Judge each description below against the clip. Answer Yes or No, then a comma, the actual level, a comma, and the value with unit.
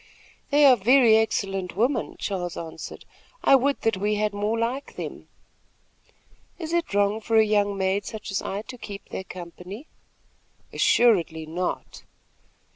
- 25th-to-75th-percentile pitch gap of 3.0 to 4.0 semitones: Yes, average, 3.6 semitones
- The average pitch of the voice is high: Yes, high, 210 Hz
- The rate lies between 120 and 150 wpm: Yes, average, 145 wpm